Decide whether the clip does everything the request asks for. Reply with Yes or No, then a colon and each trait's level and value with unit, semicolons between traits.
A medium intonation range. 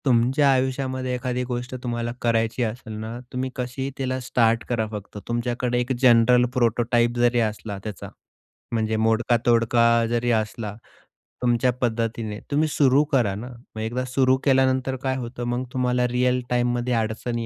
No: narrow, 1.6 semitones